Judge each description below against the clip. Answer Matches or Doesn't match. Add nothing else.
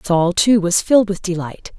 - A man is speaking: Doesn't match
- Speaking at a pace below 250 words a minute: Matches